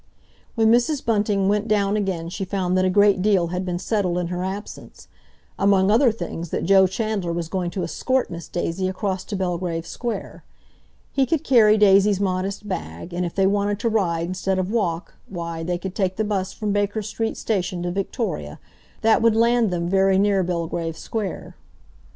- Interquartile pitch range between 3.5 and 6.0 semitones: No, average, 2.9 semitones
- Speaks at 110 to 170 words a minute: No, average, 185 wpm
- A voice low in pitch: No, high, 195 Hz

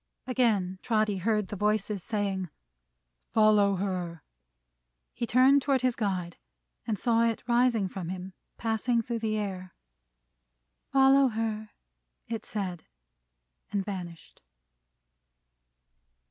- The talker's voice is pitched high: Yes, high, 215 Hz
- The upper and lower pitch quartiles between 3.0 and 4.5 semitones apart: Yes, average, 3.5 semitones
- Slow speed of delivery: Yes, slow, 105 wpm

